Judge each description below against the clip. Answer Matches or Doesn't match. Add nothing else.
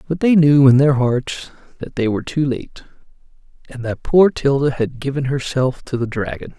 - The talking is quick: Doesn't match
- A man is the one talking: Matches